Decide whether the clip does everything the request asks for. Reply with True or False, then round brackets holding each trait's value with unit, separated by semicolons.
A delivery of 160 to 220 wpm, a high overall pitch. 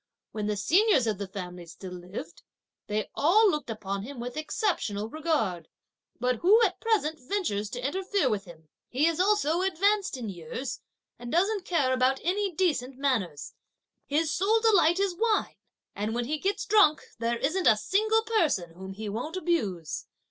True (170 wpm; 275 Hz)